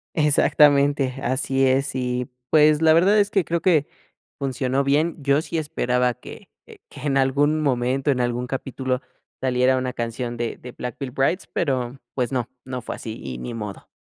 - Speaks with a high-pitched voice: No, low, 135 Hz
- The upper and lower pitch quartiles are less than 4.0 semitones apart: Yes, average, 2.8 semitones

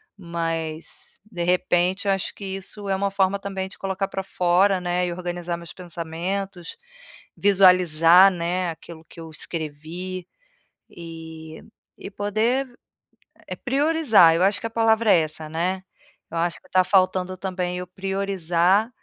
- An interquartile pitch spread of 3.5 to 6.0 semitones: No, narrow, 2.5 semitones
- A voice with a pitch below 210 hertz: Yes, medium, 185 Hz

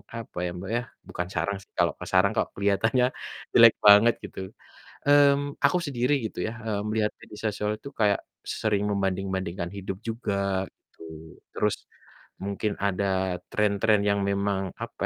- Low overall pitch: Yes, low, 105 Hz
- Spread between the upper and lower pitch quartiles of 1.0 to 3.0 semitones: Yes, narrow, 2.5 semitones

